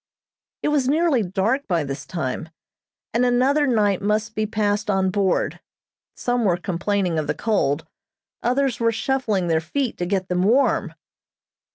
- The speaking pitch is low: No, high, 210 Hz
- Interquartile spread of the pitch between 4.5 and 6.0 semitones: Yes, average, 5.2 semitones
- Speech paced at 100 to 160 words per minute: Yes, average, 155 wpm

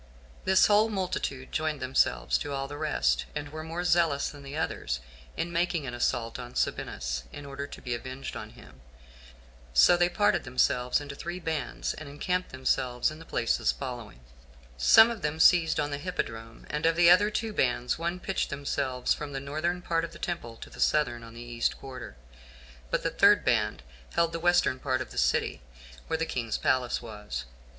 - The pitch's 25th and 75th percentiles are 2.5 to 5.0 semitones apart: No, wide, 5.5 semitones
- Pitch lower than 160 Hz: Yes, medium, 140 Hz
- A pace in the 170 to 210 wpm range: Yes, average, 190 wpm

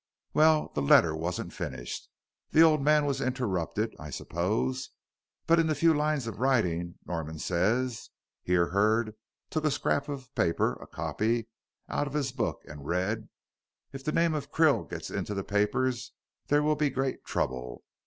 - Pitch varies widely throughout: Yes, wide, 8.2 semitones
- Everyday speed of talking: Yes, average, 165 wpm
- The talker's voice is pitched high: No, low, 125 Hz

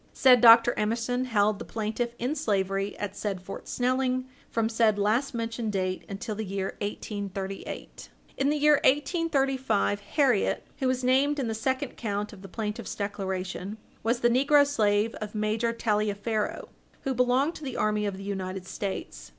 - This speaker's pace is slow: No, average, 165 wpm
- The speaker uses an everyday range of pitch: Yes, average, 4.0 semitones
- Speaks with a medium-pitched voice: No, high, 220 Hz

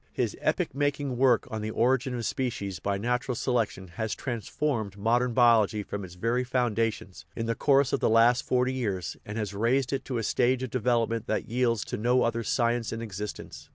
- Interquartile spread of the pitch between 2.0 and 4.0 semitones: Yes, average, 2.7 semitones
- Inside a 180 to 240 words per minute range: Yes, fast, 205 wpm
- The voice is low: Yes, low, 115 Hz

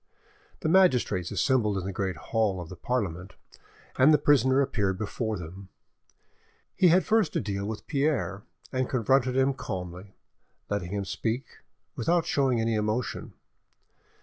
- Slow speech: No, average, 145 wpm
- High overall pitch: No, low, 110 Hz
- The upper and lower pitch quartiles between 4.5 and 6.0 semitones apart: Yes, wide, 5.4 semitones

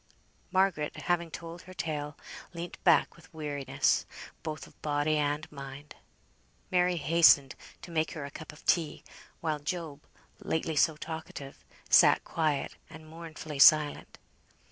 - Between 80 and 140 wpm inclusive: Yes, slow, 135 wpm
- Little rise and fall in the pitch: Yes, narrow, 2.3 semitones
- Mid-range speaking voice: Yes, medium, 155 Hz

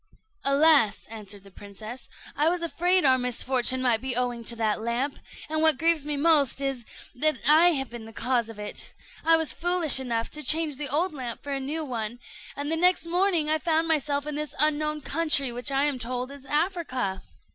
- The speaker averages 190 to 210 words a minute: Yes, average, 200 wpm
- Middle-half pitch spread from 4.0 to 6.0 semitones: Yes, average, 4.3 semitones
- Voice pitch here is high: Yes, very high, 280 Hz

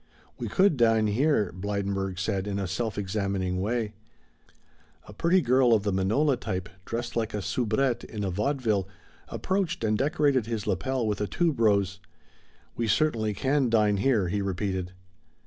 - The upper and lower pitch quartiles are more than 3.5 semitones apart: Yes, average, 4.4 semitones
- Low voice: Yes, low, 110 Hz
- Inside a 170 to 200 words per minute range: No, average, 160 wpm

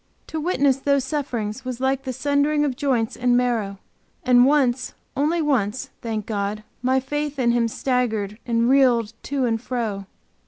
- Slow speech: No, average, 160 wpm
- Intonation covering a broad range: No, average, 3.2 semitones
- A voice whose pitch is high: Yes, very high, 250 Hz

